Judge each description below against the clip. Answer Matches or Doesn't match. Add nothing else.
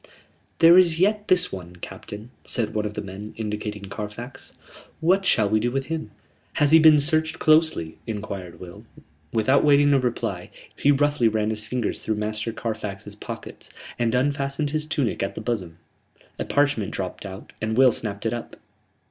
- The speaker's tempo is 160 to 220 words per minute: Matches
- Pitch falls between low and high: Doesn't match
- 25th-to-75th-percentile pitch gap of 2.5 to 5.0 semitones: Doesn't match